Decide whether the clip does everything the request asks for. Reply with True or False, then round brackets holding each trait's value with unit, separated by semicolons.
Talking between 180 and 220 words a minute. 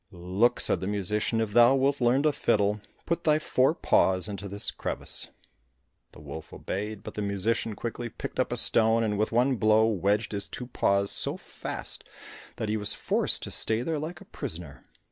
True (190 wpm)